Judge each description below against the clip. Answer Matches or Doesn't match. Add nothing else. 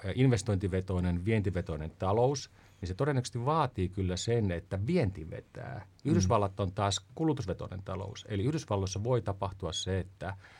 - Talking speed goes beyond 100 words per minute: Matches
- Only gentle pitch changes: Doesn't match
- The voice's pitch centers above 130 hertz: Doesn't match